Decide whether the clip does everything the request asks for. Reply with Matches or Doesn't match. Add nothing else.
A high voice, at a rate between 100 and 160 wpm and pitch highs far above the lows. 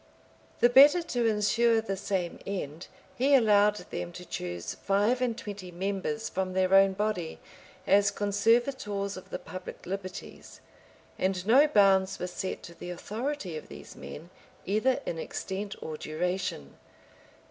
Doesn't match